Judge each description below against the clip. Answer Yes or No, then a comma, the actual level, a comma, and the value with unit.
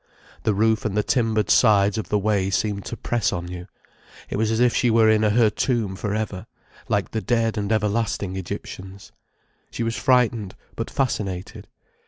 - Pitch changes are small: Yes, narrow, 2.3 semitones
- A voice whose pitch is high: No, low, 110 Hz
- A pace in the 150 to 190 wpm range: Yes, average, 180 wpm